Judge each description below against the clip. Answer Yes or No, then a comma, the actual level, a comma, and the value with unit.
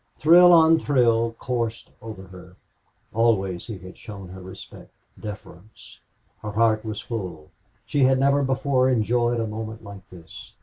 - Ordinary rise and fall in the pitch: Yes, average, 4.7 semitones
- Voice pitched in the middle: No, low, 115 Hz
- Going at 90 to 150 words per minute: Yes, average, 145 wpm